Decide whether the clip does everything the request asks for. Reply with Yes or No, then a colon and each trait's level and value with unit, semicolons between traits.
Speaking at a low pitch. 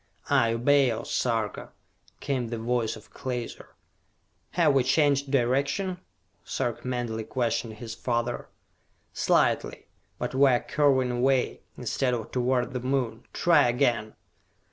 Yes: low, 125 Hz